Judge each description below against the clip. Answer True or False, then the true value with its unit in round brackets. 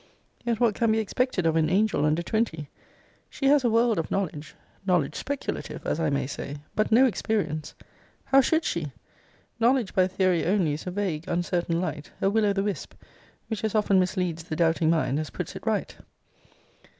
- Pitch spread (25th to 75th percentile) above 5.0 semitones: True (5.4 semitones)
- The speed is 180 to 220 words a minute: True (185 wpm)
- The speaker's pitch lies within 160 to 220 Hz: True (185 Hz)